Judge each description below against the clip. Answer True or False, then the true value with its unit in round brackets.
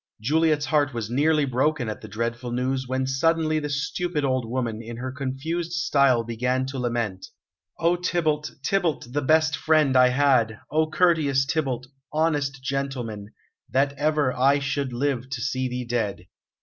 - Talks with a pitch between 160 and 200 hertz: False (135 Hz)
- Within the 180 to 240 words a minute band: False (160 wpm)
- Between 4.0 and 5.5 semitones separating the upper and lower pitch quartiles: False (3.5 semitones)